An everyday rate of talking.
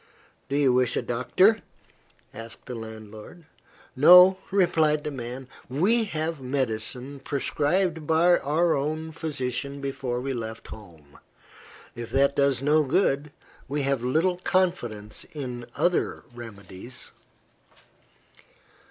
No: slow, 115 wpm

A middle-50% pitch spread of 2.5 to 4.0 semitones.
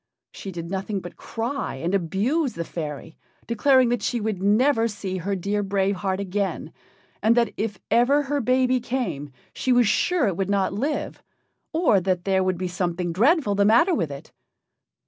No: average, 4.8 semitones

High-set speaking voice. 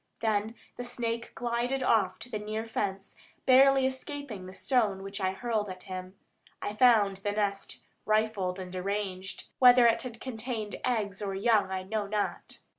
Yes: high, 215 Hz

